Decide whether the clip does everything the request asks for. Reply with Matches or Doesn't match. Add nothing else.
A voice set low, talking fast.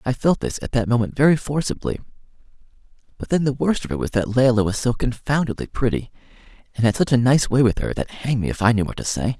Matches